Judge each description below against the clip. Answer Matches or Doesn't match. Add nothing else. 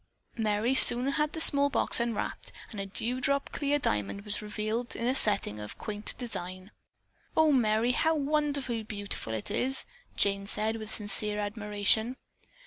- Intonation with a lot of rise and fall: Doesn't match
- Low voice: Doesn't match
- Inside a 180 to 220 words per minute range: Doesn't match